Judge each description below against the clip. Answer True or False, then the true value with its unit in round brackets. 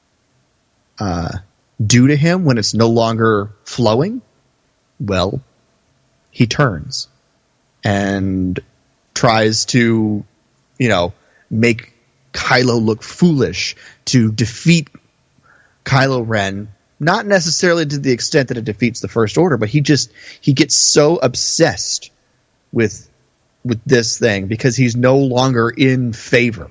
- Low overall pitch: True (120 Hz)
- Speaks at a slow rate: True (120 wpm)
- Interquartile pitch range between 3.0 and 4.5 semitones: True (3.4 semitones)